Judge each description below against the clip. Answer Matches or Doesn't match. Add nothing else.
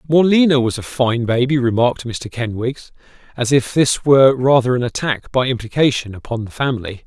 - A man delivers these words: Matches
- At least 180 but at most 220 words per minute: Doesn't match